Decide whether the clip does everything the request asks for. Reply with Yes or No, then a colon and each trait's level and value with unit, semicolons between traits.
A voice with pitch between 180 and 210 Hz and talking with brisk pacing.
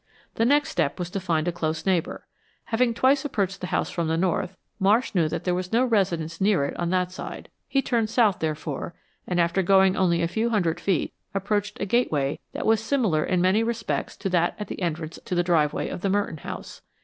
Yes: medium, 185 Hz; fast, 220 wpm